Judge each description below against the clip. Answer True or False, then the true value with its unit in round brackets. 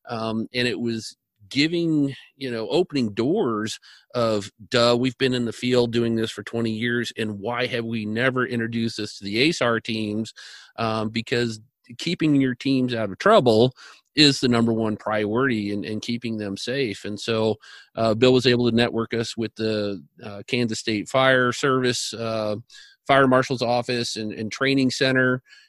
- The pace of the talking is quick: False (170 wpm)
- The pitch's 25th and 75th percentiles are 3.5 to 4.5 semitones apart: False (2.5 semitones)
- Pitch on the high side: False (115 Hz)